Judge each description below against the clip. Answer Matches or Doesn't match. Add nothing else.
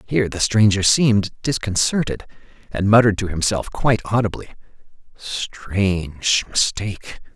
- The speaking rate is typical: Doesn't match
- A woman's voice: Doesn't match